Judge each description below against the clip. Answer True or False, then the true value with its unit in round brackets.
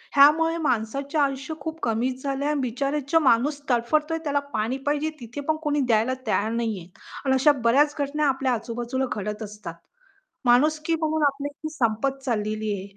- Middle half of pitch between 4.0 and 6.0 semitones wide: True (4.3 semitones)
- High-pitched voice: True (270 Hz)